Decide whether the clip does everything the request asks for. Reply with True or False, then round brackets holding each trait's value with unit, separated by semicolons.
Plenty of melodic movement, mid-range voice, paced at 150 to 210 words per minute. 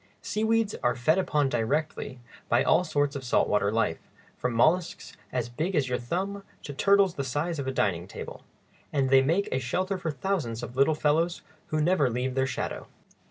True (5.8 semitones; 145 Hz; 190 wpm)